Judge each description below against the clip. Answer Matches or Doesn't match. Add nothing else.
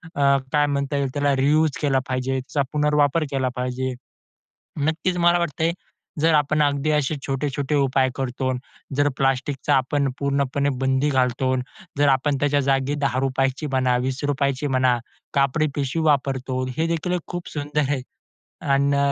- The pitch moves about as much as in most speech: Doesn't match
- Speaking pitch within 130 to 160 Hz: Matches